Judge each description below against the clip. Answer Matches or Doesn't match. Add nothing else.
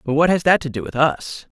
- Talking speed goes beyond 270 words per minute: Matches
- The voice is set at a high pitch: Doesn't match